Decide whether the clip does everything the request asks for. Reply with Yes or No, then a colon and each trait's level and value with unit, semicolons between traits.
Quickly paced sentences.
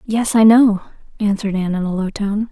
Yes: fast, 215 wpm